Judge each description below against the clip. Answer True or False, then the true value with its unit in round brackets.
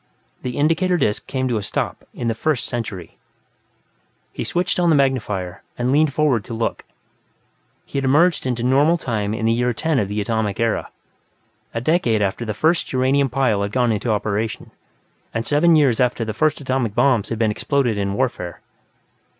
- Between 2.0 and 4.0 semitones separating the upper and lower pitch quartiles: False (4.5 semitones)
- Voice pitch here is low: True (120 Hz)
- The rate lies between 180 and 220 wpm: True (185 wpm)